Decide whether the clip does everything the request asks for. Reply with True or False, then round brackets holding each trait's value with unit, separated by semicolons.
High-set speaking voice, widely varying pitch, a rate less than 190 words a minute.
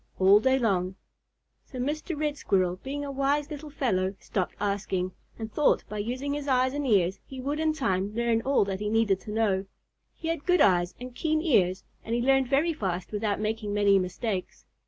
False (225 Hz; 6.3 semitones; 200 wpm)